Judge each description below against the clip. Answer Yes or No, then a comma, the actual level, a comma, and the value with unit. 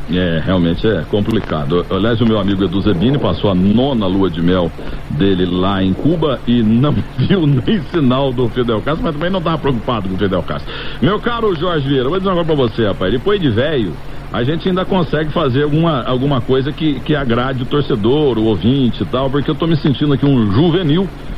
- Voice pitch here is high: No, low, 125 Hz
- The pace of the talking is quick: Yes, fast, 210 wpm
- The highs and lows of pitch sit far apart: Yes, wide, 7.1 semitones